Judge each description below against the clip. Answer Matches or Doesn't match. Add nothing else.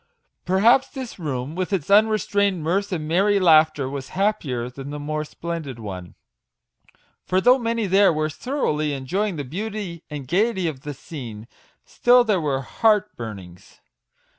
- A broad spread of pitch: Matches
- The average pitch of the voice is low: Doesn't match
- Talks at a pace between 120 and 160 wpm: Matches